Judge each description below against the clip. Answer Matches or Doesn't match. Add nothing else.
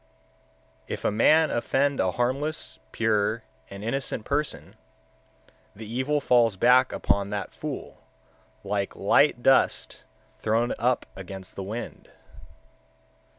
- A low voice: Matches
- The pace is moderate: Doesn't match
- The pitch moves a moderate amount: Matches